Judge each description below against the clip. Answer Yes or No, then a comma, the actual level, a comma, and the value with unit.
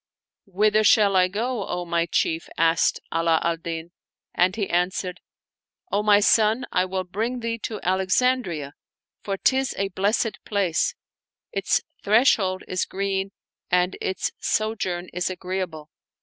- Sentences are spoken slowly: No, average, 145 wpm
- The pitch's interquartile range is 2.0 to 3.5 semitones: Yes, average, 3.1 semitones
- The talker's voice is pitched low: No, high, 190 Hz